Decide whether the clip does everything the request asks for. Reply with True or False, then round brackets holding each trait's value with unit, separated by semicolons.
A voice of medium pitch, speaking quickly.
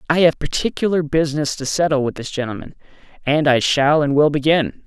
False (150 Hz; 185 wpm)